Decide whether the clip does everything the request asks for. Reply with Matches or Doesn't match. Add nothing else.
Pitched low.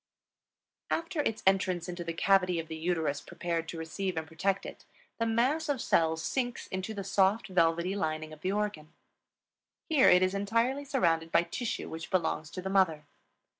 Doesn't match